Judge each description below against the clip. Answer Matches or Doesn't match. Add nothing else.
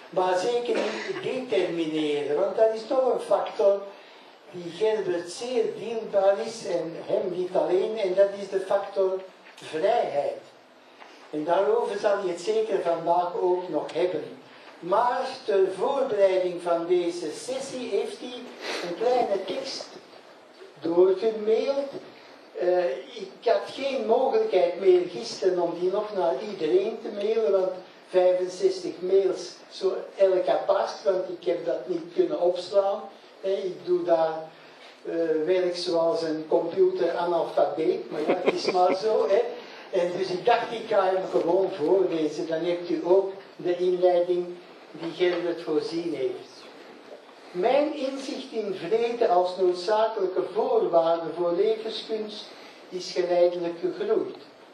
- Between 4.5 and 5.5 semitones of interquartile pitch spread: Matches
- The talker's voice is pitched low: Doesn't match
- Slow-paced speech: Matches